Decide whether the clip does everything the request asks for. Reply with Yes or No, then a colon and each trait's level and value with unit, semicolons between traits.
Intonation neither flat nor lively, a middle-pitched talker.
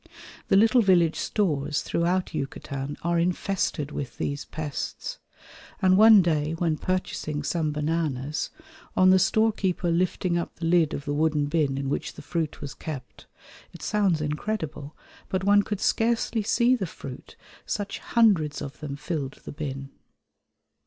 Yes: average, 4.3 semitones; medium, 165 Hz